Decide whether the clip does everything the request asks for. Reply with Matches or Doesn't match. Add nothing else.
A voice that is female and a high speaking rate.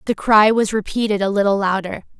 Doesn't match